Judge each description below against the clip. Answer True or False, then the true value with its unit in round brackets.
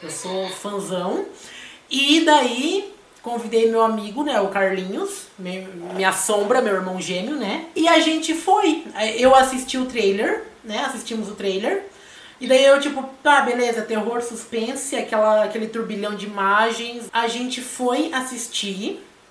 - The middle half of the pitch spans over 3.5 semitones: True (5.1 semitones)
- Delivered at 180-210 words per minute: False (150 wpm)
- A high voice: True (235 Hz)